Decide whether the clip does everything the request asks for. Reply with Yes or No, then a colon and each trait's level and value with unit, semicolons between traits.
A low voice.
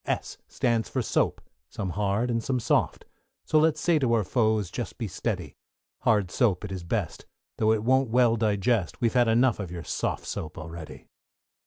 Yes: low, 110 Hz